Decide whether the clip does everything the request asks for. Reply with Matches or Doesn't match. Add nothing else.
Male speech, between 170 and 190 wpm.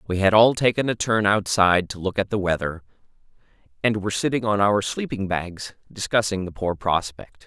Matches